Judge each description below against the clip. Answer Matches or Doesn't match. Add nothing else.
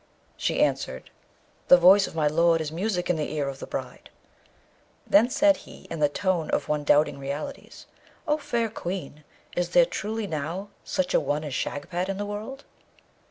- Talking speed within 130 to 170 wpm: Doesn't match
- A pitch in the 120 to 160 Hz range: Doesn't match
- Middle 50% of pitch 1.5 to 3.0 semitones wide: Doesn't match